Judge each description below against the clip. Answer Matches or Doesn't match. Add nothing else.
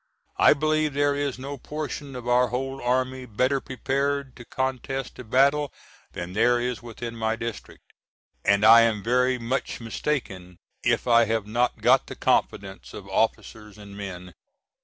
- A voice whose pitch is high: Doesn't match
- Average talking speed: Matches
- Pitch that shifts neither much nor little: Matches